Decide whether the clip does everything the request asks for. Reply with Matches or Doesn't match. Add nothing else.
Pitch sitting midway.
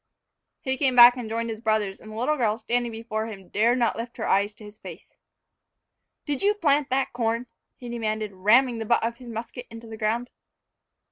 Doesn't match